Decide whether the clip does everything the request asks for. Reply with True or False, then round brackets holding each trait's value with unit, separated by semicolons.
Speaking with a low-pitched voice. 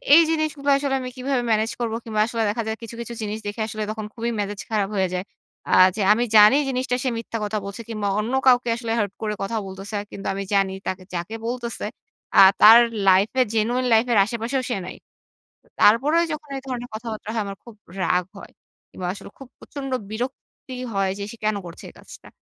False (225 Hz)